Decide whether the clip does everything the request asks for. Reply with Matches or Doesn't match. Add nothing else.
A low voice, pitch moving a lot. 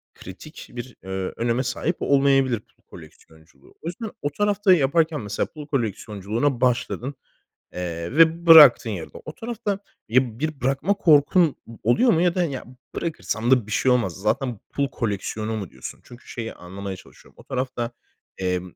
Matches